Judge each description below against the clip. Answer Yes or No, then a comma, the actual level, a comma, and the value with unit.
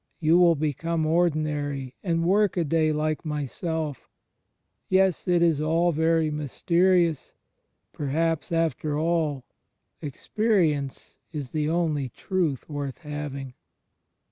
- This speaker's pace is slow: Yes, slow, 110 wpm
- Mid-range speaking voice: Yes, medium, 155 Hz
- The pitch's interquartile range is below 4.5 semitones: Yes, narrow, 2.5 semitones